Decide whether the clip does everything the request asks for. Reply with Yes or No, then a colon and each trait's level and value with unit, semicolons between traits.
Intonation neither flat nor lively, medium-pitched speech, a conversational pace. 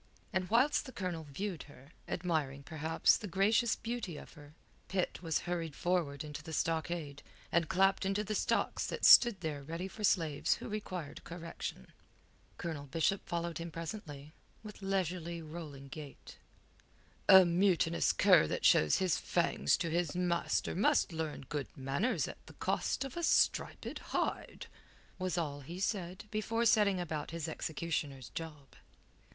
Yes: average, 3.8 semitones; medium, 170 Hz; average, 150 wpm